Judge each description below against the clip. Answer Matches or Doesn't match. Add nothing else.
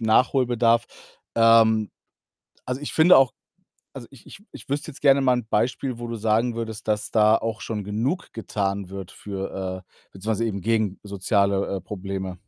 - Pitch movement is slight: Doesn't match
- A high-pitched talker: Doesn't match